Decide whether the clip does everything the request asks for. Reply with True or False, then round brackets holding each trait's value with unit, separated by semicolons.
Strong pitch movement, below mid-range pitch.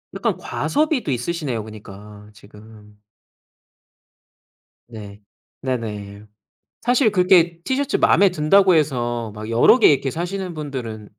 True (8.9 semitones; 130 Hz)